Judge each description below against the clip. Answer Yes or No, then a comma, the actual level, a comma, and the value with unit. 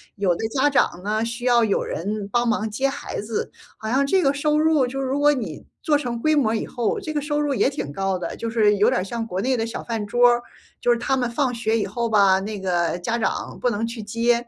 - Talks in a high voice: Yes, high, 235 Hz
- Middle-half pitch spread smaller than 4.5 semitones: Yes, average, 4.0 semitones